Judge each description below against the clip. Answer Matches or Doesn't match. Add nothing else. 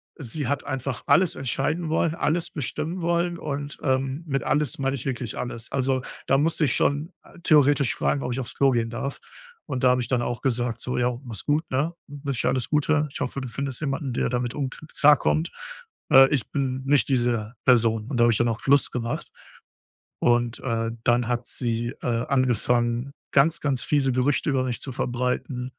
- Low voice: Matches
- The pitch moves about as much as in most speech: Matches